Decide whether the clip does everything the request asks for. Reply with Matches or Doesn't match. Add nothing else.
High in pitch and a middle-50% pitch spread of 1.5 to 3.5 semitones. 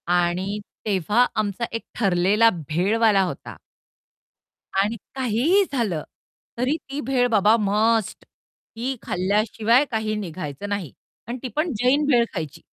Doesn't match